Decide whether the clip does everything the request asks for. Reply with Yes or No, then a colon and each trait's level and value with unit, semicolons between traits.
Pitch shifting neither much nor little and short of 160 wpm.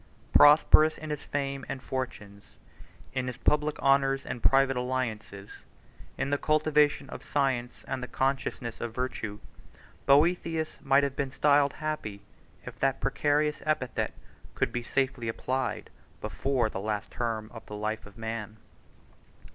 Yes: average, 3.7 semitones; average, 140 wpm